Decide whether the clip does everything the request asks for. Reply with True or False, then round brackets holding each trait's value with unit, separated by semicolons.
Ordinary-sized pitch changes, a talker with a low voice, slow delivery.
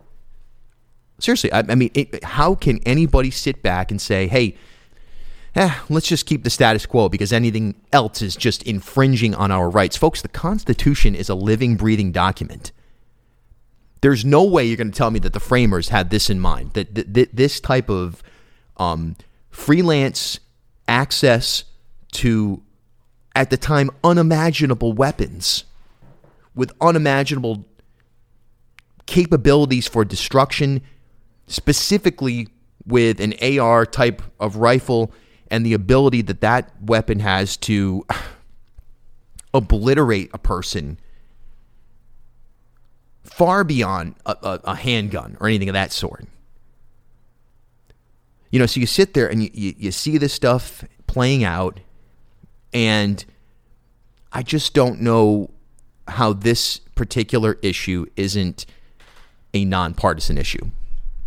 True (3.5 semitones; 115 Hz; 125 wpm)